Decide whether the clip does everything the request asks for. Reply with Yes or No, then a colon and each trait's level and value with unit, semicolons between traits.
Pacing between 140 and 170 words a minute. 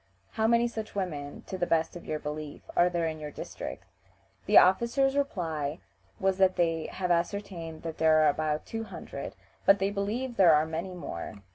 No: average, 180 wpm